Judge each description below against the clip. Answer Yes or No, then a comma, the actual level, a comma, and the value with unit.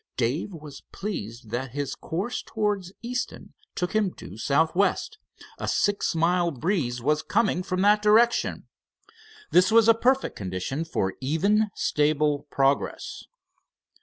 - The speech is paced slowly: Yes, slow, 130 wpm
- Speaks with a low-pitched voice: No, medium, 170 Hz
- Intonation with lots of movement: Yes, wide, 7.0 semitones